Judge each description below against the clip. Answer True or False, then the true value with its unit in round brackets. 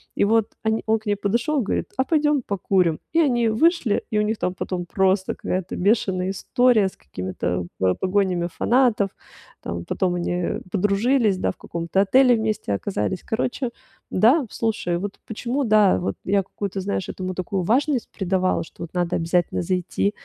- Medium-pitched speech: False (200 Hz)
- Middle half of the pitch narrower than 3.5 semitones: False (3.8 semitones)